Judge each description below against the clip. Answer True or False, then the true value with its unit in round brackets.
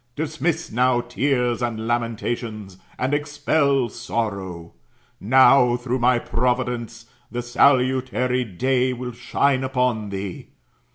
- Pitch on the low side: True (125 Hz)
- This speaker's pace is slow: True (105 wpm)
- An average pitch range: False (2.0 semitones)